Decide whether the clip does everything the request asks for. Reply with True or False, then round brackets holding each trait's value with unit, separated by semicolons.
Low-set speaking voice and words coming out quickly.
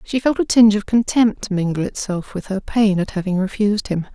False (205 Hz; 215 wpm)